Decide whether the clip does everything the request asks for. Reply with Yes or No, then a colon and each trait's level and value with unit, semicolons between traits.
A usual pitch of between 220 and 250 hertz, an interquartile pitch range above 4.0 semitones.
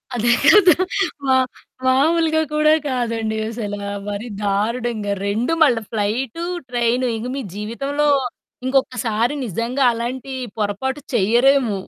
No: high, 240 Hz; average, 3.7 semitones